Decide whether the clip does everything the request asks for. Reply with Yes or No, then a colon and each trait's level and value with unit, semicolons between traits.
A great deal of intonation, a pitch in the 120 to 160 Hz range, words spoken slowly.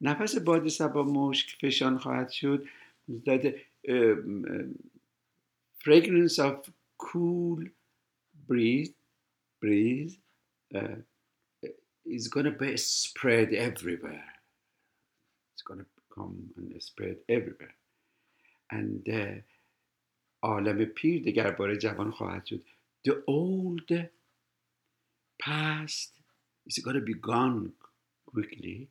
Yes: wide, 6.1 semitones; medium, 140 Hz; slow, 90 wpm